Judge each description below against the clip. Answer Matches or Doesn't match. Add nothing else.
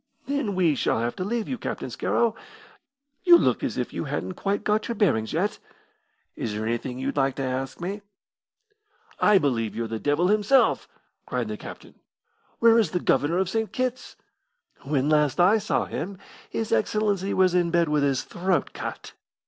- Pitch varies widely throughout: Matches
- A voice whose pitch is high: Doesn't match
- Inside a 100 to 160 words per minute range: Doesn't match